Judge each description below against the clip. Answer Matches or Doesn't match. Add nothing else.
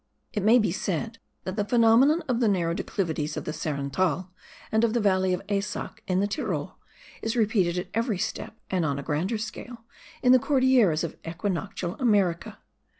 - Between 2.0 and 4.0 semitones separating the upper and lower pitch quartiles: Doesn't match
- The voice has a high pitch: Matches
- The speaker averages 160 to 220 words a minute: Matches